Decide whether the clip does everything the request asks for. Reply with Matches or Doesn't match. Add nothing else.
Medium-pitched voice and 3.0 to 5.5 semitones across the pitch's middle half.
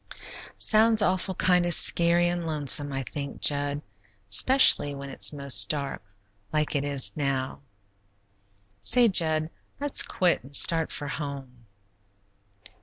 Matches